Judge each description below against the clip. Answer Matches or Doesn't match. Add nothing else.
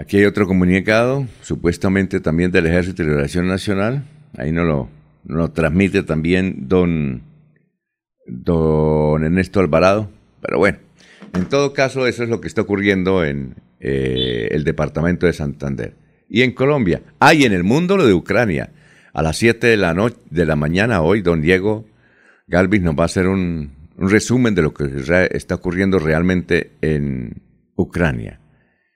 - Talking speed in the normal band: Matches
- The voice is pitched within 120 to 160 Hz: Doesn't match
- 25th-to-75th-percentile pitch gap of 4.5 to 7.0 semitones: Matches